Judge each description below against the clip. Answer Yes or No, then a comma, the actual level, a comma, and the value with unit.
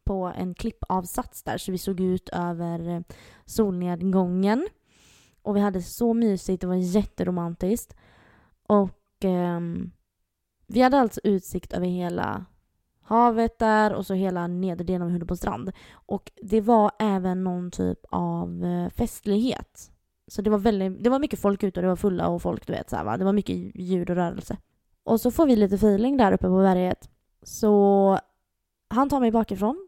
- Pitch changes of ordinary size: Yes, average, 3.3 semitones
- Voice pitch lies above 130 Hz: Yes, high, 190 Hz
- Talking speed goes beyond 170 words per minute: No, average, 165 wpm